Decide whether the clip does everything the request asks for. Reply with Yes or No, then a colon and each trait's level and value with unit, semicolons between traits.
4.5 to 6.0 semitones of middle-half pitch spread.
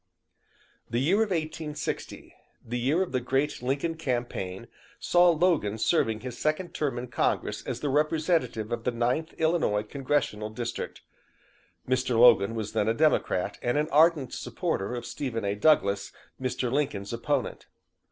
Yes: average, 5.2 semitones